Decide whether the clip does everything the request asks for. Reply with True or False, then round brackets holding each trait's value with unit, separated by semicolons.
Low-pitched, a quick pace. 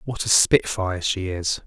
False (95 Hz; 180 wpm)